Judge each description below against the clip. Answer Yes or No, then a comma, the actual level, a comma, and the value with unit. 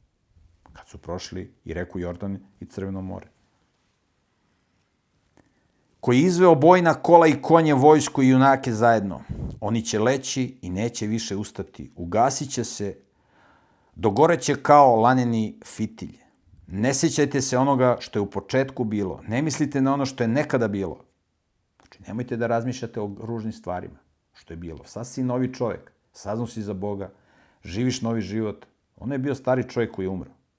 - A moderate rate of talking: Yes, average, 160 wpm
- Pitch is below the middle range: Yes, low, 115 Hz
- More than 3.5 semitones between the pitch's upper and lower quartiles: Yes, average, 4.9 semitones